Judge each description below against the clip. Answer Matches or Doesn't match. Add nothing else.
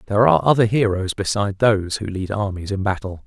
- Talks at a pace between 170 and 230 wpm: Matches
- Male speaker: Matches